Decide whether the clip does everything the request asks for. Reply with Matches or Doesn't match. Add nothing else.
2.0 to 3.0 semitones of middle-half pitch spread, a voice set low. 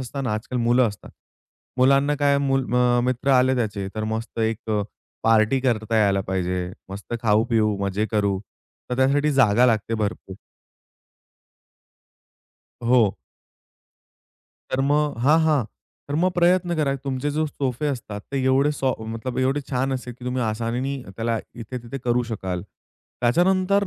Doesn't match